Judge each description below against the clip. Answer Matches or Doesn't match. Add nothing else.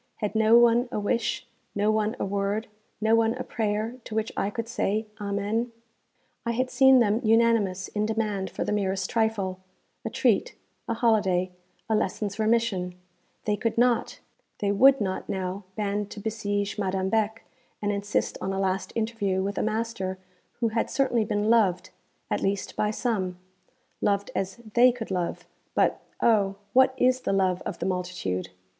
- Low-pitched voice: Doesn't match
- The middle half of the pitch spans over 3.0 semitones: Doesn't match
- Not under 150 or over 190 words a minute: Matches